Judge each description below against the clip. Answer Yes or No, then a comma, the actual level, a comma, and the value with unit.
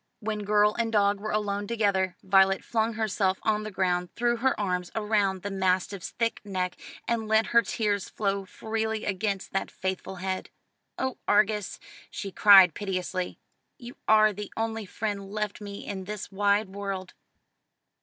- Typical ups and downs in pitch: No, narrow, 2.1 semitones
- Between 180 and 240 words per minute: No, average, 155 wpm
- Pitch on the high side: Yes, high, 205 Hz